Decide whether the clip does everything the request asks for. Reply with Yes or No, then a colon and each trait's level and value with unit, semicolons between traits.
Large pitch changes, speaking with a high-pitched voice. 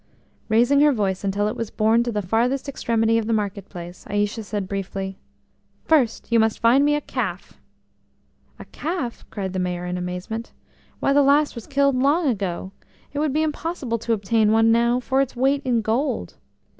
No: average, 5.0 semitones; high, 230 Hz